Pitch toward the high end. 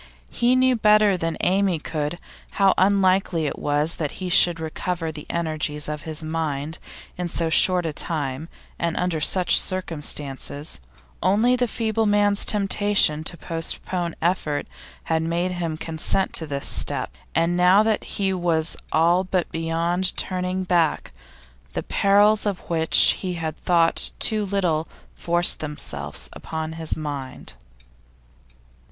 No: medium, 170 Hz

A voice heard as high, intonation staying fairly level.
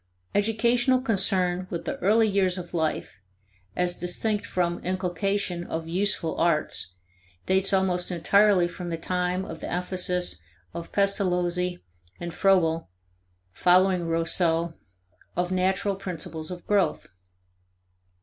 No: medium, 180 Hz; narrow, 2.1 semitones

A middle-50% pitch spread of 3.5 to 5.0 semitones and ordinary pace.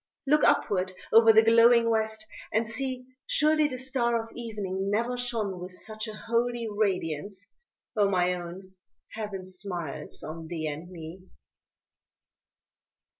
No: average, 4.1 semitones; slow, 130 wpm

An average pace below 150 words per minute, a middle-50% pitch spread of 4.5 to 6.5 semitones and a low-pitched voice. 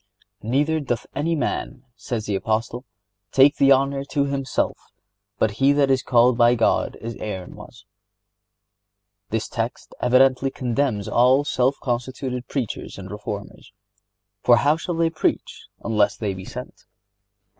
Yes: average, 140 wpm; average, 4.8 semitones; low, 120 Hz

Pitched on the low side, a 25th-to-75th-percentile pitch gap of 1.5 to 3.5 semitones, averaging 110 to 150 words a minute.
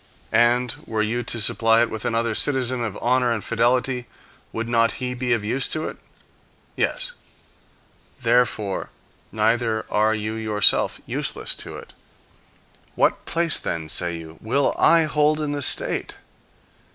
Yes: low, 115 Hz; average, 2.7 semitones; average, 145 wpm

